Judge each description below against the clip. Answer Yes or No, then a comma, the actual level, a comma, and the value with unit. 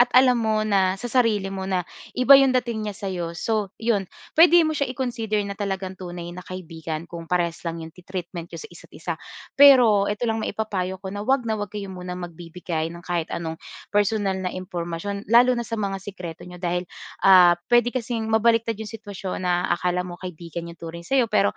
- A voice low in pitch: No, high, 195 Hz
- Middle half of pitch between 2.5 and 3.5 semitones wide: No, average, 4.0 semitones